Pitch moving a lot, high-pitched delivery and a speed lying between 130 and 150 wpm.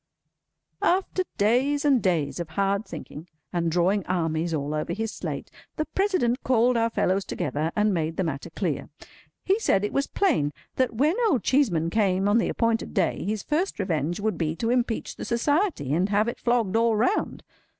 No: wide, 6.5 semitones; high, 210 Hz; average, 180 wpm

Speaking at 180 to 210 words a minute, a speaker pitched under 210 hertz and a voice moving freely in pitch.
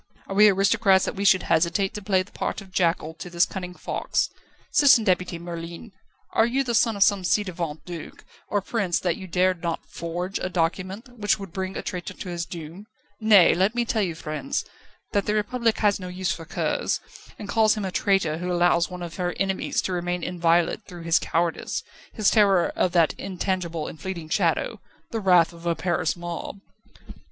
No: average, 200 wpm; medium, 185 Hz; average, 2.9 semitones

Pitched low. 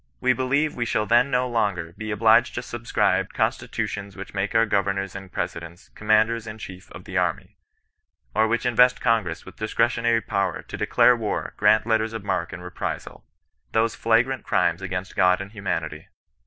Yes: low, 110 Hz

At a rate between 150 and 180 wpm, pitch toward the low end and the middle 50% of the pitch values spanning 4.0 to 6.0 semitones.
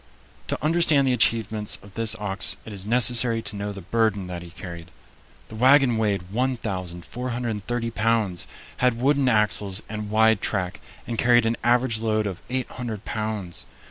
No: average, 155 wpm; low, 110 Hz; average, 3.1 semitones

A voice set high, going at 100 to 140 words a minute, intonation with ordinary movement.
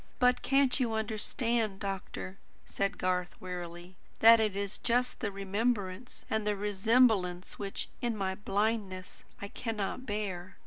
Yes: high, 205 Hz; slow, 135 wpm; average, 3.3 semitones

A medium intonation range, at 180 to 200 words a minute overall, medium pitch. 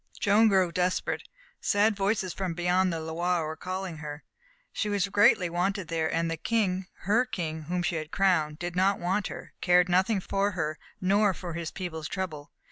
Yes: average, 3.0 semitones; average, 185 wpm; medium, 180 Hz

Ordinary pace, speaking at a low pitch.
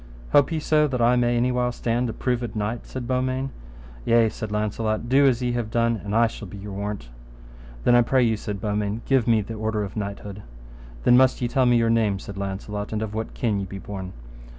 No: fast, 230 wpm; low, 115 Hz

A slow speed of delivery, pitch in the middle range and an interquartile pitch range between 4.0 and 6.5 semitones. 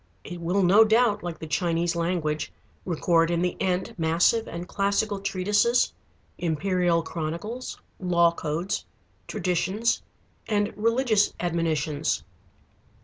No: slow, 110 wpm; medium, 180 Hz; average, 3.5 semitones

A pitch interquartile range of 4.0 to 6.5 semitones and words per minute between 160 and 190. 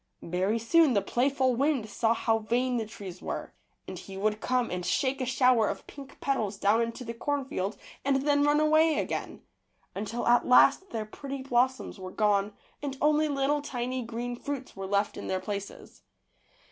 Yes: average, 4.4 semitones; average, 180 wpm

